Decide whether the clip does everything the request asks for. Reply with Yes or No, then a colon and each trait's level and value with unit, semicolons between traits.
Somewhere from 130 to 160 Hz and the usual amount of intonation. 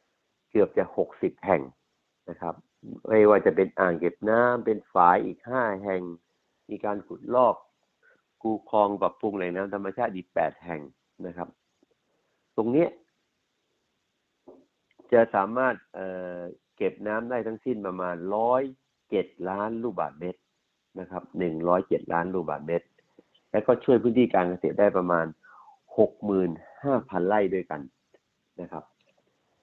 No: very low, 95 Hz; average, 3.9 semitones